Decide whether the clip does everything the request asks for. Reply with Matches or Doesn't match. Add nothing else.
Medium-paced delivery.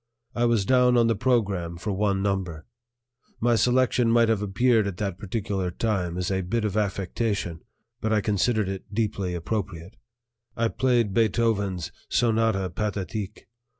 Matches